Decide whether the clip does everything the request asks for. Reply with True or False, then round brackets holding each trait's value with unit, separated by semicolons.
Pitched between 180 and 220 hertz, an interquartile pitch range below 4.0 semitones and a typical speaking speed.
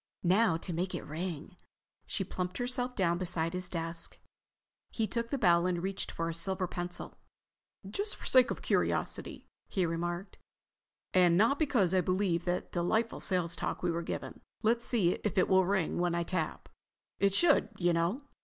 True (185 Hz; 3.2 semitones; 180 wpm)